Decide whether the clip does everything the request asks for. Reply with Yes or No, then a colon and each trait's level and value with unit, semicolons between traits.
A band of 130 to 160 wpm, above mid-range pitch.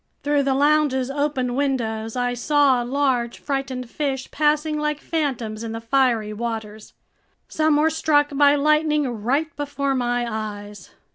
Yes: average, 140 wpm; very high, 270 Hz